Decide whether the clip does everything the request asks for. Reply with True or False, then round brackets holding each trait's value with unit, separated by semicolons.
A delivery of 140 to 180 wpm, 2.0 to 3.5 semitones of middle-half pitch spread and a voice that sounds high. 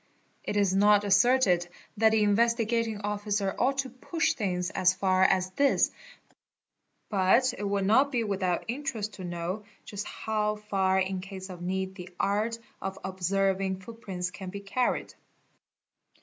True (150 wpm; 2.8 semitones; 200 Hz)